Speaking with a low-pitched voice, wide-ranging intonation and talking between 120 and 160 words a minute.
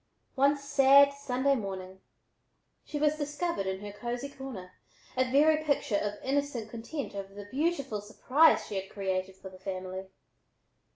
No: very high, 250 Hz; wide, 6.3 semitones; average, 150 wpm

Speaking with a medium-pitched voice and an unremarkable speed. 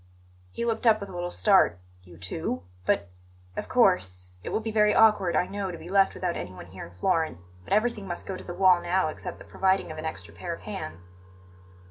No: medium, 175 Hz; fast, 225 wpm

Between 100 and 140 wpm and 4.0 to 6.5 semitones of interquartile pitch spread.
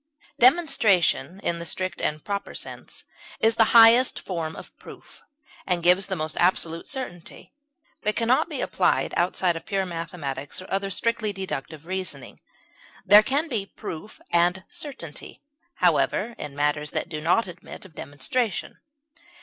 No: average, 150 wpm; average, 4.5 semitones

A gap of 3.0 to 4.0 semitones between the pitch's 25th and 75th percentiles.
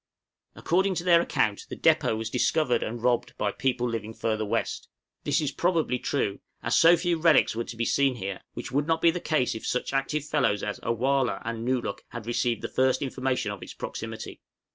No: average, 5.2 semitones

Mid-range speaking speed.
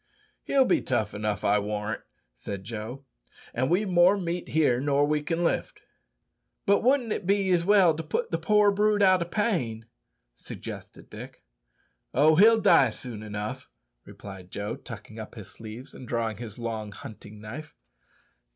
Yes: average, 160 wpm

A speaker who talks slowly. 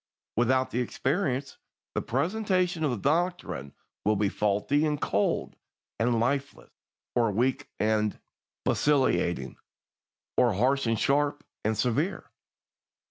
Yes: slow, 115 wpm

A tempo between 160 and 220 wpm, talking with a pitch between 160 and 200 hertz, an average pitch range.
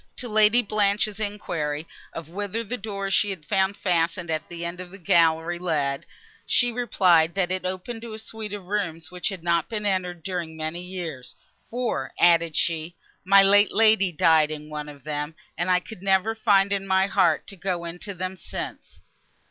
Yes: average, 190 wpm; medium, 185 Hz; average, 3.5 semitones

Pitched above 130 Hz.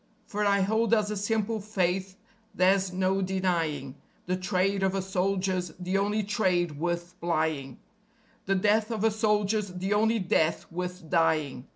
Yes: high, 190 Hz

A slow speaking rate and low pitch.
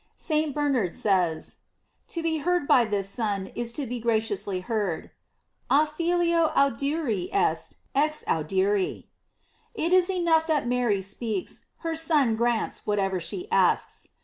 No: slow, 130 wpm; high, 245 Hz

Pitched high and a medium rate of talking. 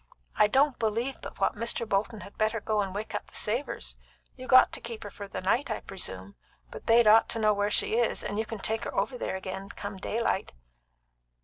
No: high, 215 Hz; fast, 225 wpm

